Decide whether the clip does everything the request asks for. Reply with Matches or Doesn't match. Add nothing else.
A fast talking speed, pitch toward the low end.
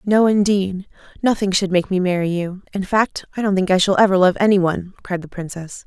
Doesn't match